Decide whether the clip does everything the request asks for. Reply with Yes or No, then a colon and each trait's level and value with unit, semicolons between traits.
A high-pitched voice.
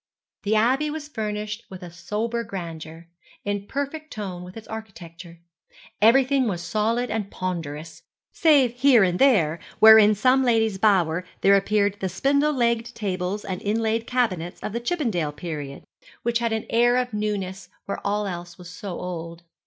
Yes: high, 210 Hz